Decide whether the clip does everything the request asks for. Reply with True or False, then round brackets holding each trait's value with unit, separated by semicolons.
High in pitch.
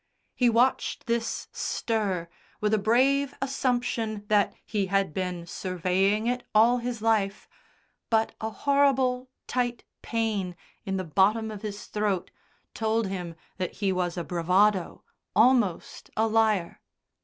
True (215 Hz)